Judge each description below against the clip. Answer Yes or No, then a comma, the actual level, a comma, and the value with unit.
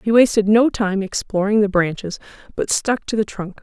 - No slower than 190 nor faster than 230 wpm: Yes, average, 200 wpm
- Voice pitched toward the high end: Yes, high, 205 Hz